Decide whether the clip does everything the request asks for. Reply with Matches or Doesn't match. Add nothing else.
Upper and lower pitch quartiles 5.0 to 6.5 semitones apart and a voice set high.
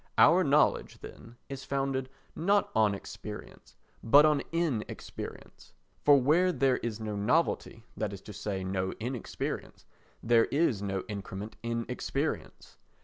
Doesn't match